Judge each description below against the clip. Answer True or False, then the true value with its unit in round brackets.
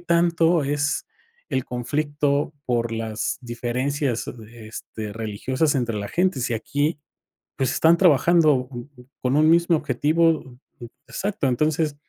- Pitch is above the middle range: False (140 Hz)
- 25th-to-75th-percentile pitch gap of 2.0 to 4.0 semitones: False (4.7 semitones)